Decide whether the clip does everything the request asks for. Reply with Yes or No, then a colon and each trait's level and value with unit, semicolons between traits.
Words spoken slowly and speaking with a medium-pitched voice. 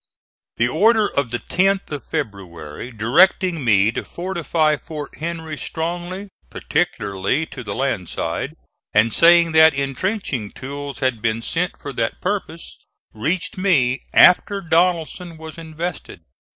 Yes: slow, 130 wpm; medium, 155 Hz